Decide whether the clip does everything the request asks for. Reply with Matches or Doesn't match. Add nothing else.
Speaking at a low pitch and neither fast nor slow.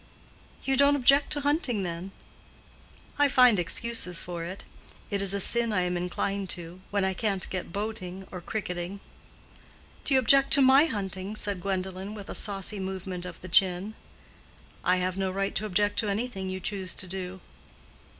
Doesn't match